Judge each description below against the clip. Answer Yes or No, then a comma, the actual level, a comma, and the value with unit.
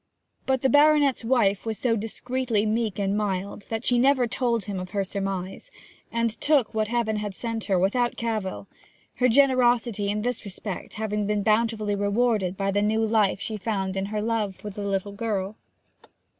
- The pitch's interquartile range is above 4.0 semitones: No, average, 2.7 semitones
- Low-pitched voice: No, high, 215 Hz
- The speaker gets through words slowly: No, average, 180 wpm